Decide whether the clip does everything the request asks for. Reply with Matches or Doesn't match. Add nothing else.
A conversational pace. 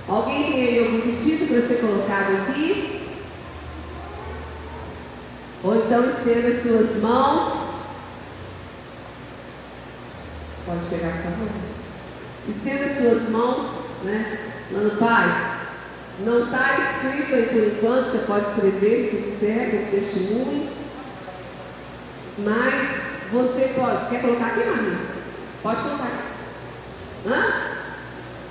Doesn't match